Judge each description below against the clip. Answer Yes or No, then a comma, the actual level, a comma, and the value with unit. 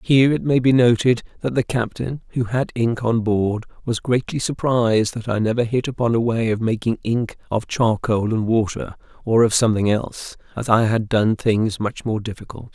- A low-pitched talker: Yes, low, 115 Hz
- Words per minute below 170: No, average, 200 wpm